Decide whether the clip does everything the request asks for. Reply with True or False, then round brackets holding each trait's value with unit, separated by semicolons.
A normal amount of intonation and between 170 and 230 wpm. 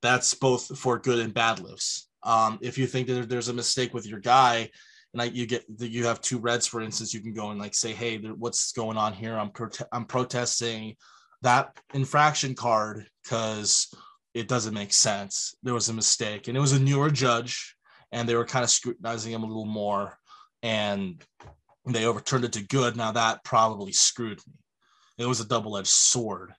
False (2.1 semitones; 200 wpm)